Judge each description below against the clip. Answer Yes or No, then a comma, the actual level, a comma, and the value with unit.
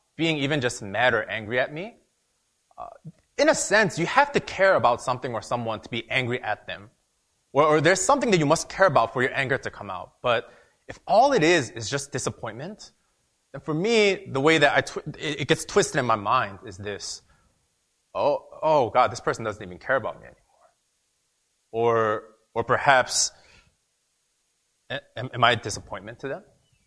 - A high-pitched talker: No, medium, 140 Hz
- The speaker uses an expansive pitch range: Yes, wide, 5.9 semitones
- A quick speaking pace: No, average, 190 wpm